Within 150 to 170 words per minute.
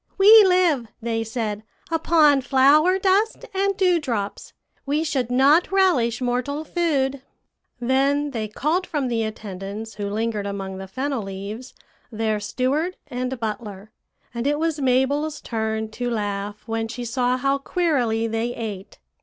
No: average, 140 wpm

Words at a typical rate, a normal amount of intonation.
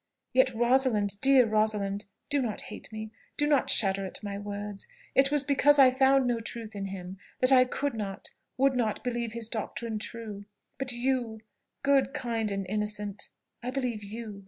Yes: average, 175 wpm; average, 3.9 semitones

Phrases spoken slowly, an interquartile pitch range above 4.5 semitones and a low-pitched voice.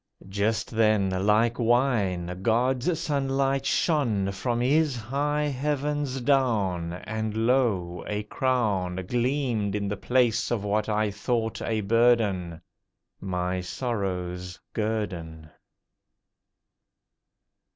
Yes: slow, 100 wpm; average, 4.9 semitones; low, 110 Hz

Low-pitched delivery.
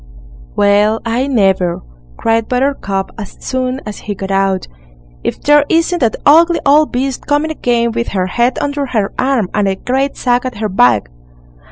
No: high, 235 Hz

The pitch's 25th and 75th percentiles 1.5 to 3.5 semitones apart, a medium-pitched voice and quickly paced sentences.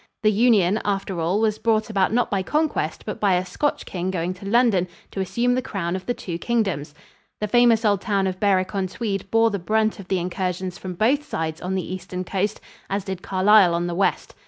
No: average, 3.0 semitones; high, 195 Hz; fast, 220 wpm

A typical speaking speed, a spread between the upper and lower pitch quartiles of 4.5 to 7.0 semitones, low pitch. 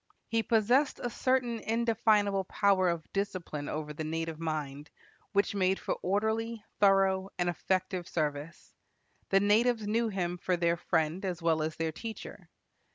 No: average, 150 wpm; average, 4.9 semitones; high, 190 Hz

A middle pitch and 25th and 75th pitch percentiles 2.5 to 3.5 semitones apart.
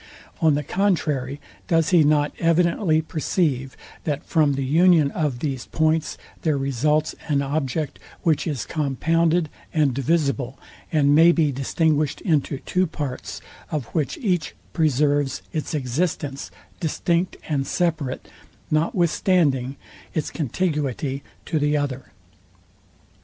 Yes: medium, 150 Hz; average, 3.0 semitones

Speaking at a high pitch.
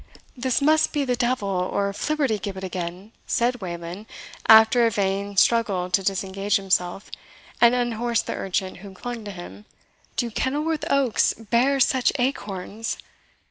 Yes: high, 215 Hz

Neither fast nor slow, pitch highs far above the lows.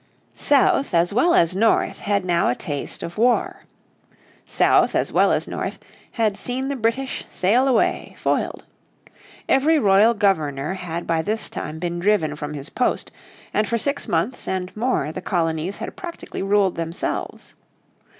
Yes: average, 160 wpm; wide, 5.9 semitones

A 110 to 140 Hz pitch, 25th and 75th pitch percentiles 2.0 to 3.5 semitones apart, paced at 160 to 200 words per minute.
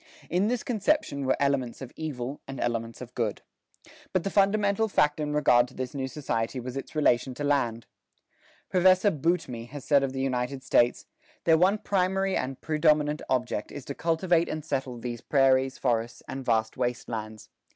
No: low, 135 Hz; average, 4.8 semitones; average, 175 wpm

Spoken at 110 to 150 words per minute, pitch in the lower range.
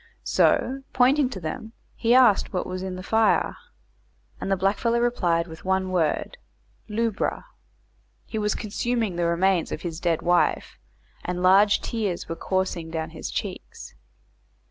No: average, 145 wpm; high, 190 Hz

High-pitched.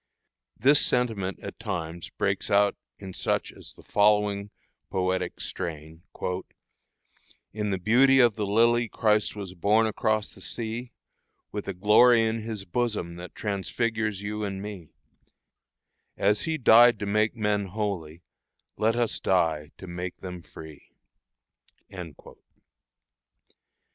No: low, 105 Hz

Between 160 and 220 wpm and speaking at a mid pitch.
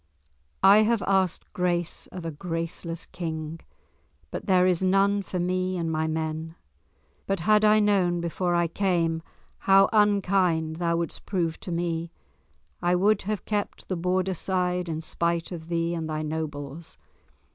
No: average, 150 wpm; medium, 175 Hz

